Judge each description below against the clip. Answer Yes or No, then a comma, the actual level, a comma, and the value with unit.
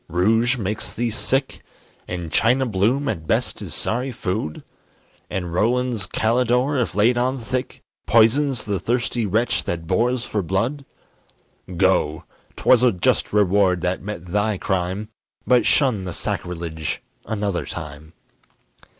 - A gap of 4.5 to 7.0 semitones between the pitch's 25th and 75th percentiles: Yes, average, 5.2 semitones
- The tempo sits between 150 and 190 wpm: No, slow, 135 wpm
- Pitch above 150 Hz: No, low, 105 Hz